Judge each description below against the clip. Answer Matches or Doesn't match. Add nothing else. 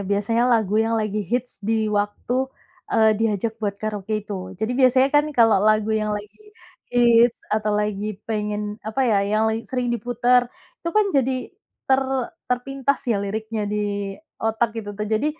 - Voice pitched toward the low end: Doesn't match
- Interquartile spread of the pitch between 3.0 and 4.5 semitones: Doesn't match